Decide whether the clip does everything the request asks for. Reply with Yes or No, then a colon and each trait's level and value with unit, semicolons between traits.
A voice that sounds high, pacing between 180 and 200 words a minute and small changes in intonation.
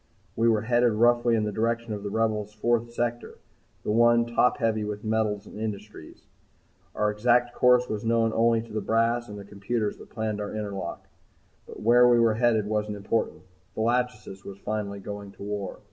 No: low, 110 Hz; average, 185 wpm; narrow, 2.1 semitones